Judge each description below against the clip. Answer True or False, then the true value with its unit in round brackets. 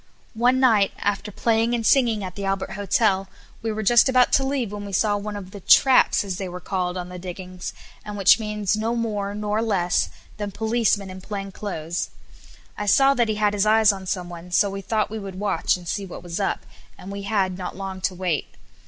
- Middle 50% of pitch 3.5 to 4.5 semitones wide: False (2.6 semitones)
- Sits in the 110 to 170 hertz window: False (205 Hz)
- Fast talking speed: True (220 wpm)